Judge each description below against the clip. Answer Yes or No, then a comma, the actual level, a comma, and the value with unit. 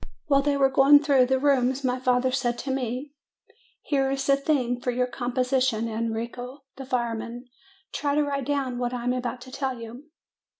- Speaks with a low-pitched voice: No, very high, 255 Hz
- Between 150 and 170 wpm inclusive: No, average, 185 wpm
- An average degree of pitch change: No, narrow, 2.0 semitones